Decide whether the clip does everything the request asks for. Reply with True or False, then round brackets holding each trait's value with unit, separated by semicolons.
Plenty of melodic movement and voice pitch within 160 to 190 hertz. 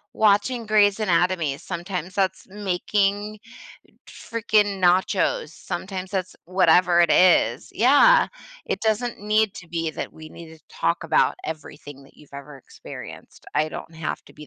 False (4.4 semitones; 185 Hz)